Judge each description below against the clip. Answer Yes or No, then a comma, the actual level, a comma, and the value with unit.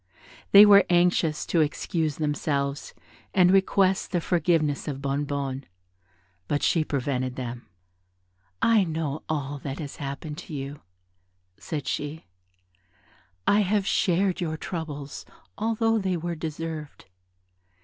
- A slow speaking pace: Yes, slow, 120 wpm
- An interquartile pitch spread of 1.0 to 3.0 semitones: No, average, 4.0 semitones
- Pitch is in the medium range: Yes, medium, 155 Hz